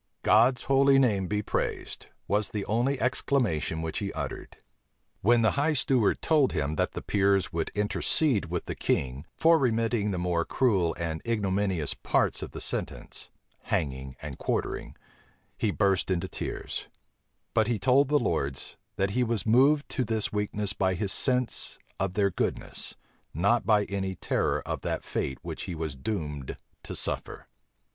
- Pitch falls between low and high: No, low, 105 Hz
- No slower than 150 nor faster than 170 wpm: Yes, average, 160 wpm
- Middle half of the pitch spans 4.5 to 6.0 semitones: Yes, wide, 5.5 semitones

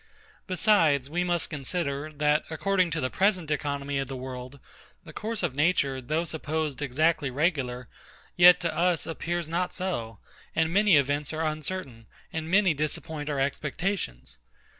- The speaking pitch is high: No, medium, 155 Hz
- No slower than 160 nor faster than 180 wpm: No, average, 150 wpm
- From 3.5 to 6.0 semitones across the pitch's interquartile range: Yes, average, 3.9 semitones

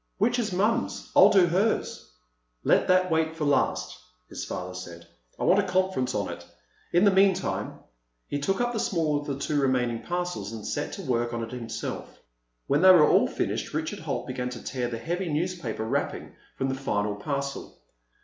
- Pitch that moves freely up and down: Yes, wide, 7.1 semitones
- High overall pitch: No, medium, 150 Hz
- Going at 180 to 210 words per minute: Yes, average, 190 wpm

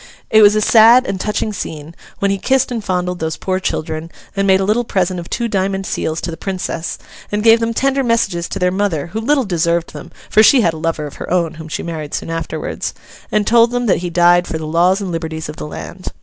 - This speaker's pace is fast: Yes, fast, 245 wpm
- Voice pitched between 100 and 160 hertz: No, medium, 185 Hz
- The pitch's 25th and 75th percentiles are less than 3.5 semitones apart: No, average, 4.7 semitones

